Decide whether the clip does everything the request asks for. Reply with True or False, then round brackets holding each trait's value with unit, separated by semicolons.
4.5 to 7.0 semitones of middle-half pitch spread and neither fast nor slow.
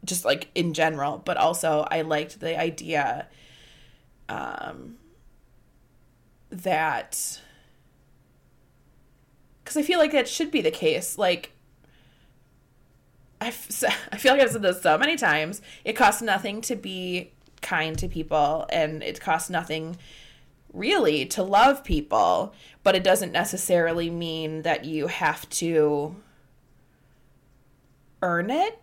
False (5.3 semitones; 125 wpm)